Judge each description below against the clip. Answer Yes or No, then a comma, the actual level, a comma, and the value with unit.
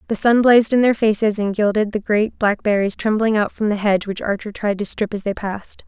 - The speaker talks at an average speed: No, fast, 245 wpm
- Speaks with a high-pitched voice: Yes, high, 210 Hz